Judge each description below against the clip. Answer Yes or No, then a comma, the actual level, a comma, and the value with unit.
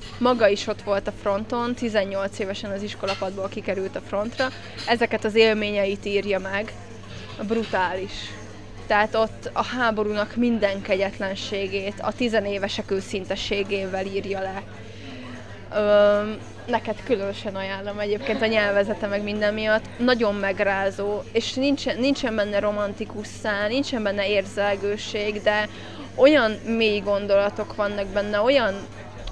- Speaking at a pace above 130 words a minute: No, average, 120 wpm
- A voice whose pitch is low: No, high, 205 Hz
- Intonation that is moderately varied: No, narrow, 1.7 semitones